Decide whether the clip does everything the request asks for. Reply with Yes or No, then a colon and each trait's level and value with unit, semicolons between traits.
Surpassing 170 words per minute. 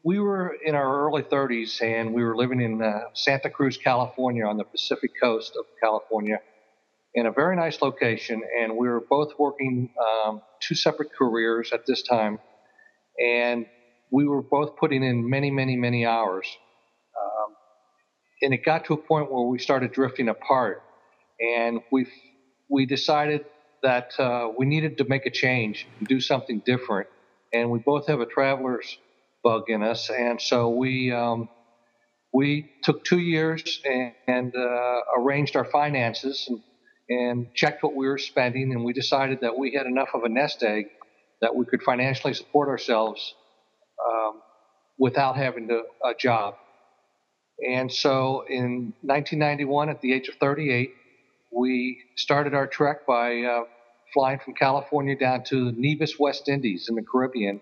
No: average, 160 wpm